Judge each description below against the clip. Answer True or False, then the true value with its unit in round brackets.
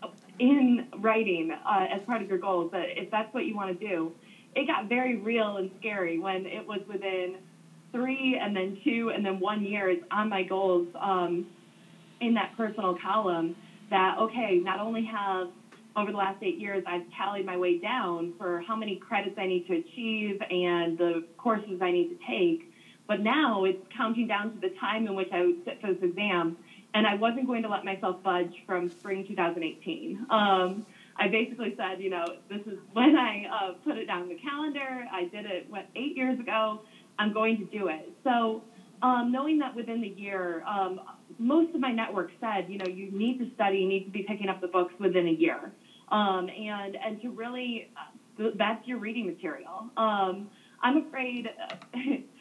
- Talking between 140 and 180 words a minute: False (195 wpm)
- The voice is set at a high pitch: True (205 Hz)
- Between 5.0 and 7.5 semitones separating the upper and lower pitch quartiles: False (3.9 semitones)